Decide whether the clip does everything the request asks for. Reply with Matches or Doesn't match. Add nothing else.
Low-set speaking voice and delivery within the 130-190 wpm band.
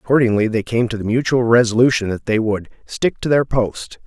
Doesn't match